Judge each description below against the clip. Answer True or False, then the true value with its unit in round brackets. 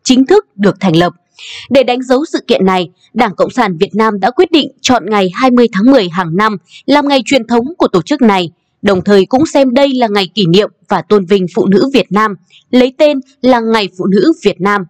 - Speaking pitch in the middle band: False (215 Hz)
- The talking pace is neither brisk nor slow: True (235 wpm)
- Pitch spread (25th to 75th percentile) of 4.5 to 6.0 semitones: True (5.4 semitones)